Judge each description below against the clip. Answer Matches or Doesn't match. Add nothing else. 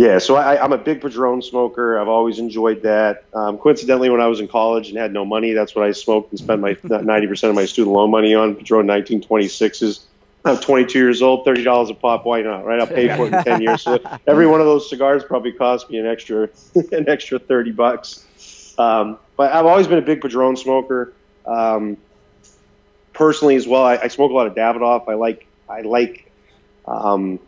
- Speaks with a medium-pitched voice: Doesn't match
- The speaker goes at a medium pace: Doesn't match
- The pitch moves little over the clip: Doesn't match